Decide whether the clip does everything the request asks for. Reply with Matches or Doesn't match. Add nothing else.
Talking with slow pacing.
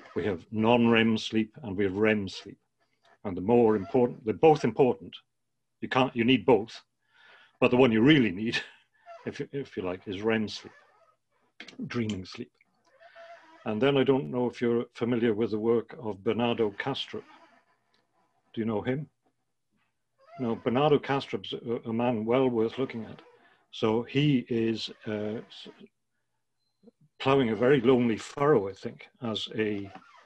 Doesn't match